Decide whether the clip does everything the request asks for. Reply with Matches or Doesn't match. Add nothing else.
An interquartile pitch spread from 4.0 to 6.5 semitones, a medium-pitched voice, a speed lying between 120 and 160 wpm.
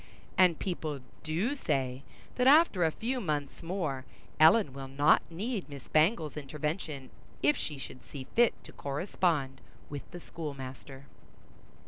Matches